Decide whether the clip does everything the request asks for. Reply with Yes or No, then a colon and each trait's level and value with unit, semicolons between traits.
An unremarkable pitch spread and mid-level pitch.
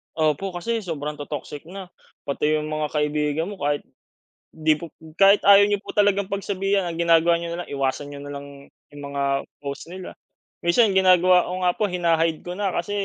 Yes: average, 4.2 semitones; medium, 170 Hz